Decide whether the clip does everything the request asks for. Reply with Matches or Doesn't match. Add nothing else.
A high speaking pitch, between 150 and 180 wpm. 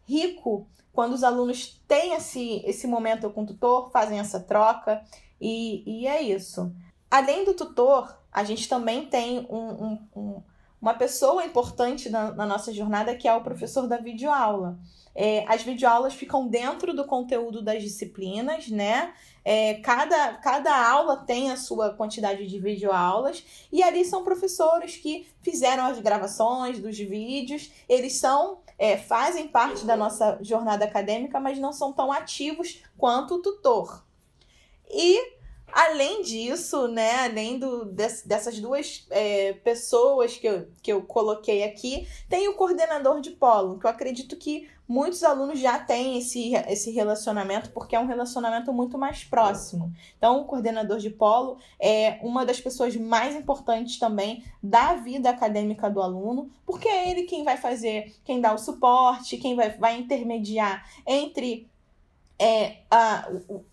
Matches